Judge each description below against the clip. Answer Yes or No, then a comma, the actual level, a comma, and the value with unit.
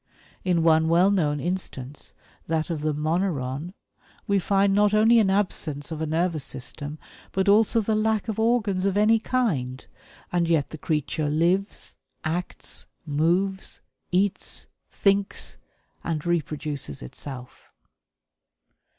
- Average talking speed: No, slow, 125 wpm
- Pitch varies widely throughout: No, average, 4.8 semitones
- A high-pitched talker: No, medium, 175 Hz